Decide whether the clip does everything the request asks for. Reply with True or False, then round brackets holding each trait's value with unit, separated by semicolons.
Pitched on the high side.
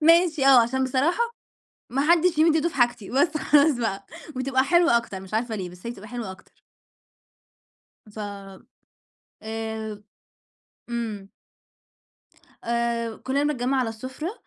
True (255 Hz)